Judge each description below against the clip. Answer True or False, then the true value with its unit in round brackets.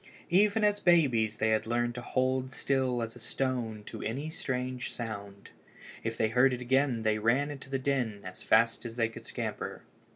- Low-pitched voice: True (125 Hz)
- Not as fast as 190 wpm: False (195 wpm)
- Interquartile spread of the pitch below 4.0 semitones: True (3.0 semitones)